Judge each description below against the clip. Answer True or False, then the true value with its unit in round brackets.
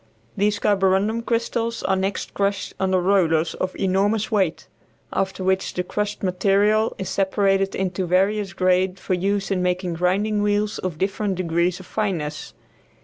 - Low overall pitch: False (190 Hz)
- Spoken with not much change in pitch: True (2.0 semitones)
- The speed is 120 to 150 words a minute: True (145 wpm)